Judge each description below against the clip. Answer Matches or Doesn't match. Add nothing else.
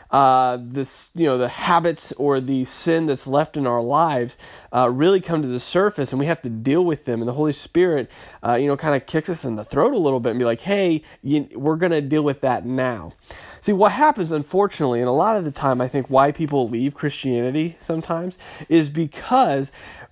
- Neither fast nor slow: Doesn't match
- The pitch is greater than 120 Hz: Matches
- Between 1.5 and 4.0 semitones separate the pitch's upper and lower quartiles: Doesn't match